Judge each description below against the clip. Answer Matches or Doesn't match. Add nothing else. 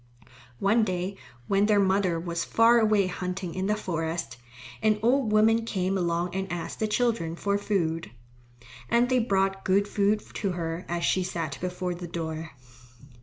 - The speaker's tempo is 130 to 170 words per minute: Matches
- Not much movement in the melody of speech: Doesn't match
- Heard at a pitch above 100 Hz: Matches